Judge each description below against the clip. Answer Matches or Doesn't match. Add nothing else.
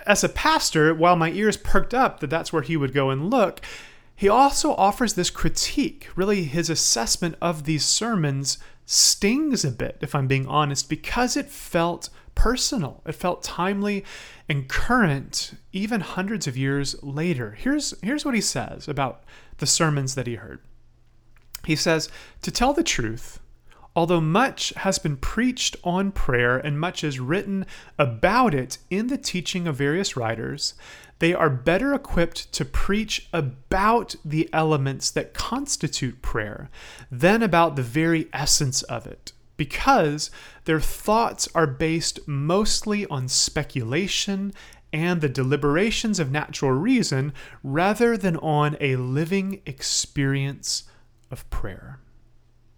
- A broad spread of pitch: Matches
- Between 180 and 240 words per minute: Doesn't match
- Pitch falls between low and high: Matches